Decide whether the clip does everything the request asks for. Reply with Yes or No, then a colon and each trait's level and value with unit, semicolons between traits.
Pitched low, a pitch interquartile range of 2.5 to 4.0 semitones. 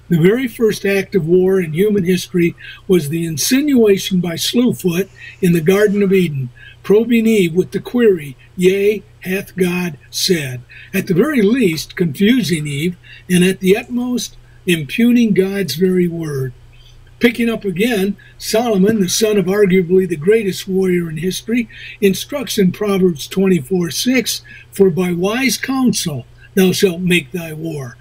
No: medium, 185 Hz; average, 3.5 semitones